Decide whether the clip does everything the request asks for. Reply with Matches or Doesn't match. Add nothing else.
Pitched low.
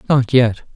Matches